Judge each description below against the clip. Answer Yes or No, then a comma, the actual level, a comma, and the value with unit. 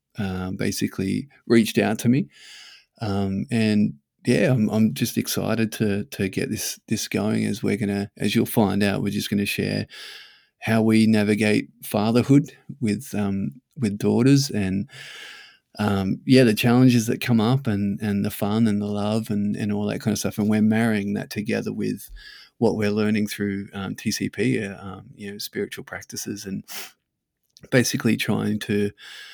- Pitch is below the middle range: Yes, low, 105 Hz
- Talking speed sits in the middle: Yes, average, 170 wpm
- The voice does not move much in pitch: Yes, narrow, 2.0 semitones